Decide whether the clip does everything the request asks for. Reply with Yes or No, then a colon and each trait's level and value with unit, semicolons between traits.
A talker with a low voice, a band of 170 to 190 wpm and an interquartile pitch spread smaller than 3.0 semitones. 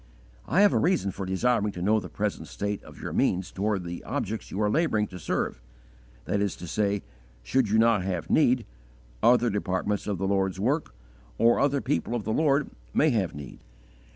No: low, 105 Hz; average, 180 wpm; average, 4.6 semitones